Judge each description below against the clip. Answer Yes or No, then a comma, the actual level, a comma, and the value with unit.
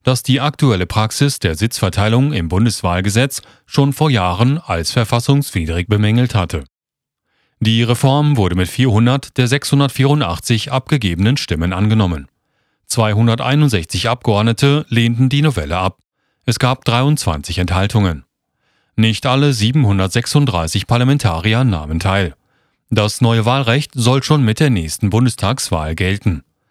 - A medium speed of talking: No, slow, 115 wpm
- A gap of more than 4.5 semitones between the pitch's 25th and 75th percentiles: Yes, average, 5.3 semitones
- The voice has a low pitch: Yes, low, 115 Hz